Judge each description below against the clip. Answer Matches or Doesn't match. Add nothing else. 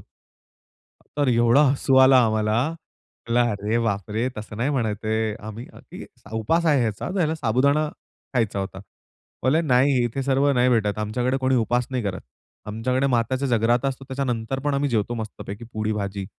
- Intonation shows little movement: Doesn't match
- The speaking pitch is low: Matches